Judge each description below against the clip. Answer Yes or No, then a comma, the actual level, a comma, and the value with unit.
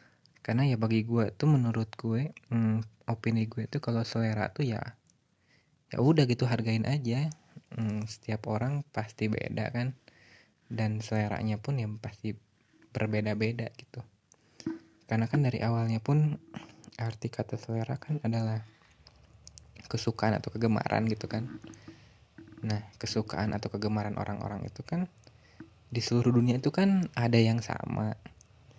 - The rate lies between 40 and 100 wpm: No, average, 130 wpm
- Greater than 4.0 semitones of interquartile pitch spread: No, narrow, 2.6 semitones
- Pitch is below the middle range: Yes, low, 115 Hz